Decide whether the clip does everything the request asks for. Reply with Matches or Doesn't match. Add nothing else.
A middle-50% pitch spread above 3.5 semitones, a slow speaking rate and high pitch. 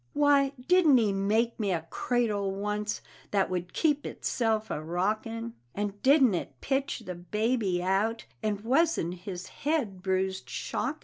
Doesn't match